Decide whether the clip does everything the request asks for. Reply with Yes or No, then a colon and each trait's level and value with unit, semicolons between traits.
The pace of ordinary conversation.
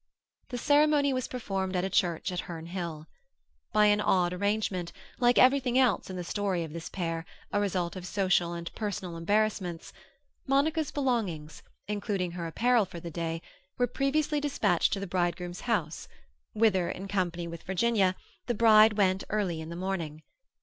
Yes: average, 160 wpm